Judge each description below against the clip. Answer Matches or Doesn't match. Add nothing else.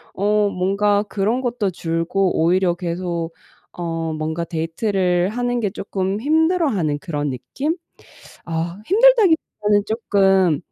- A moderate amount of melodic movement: Matches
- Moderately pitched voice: Doesn't match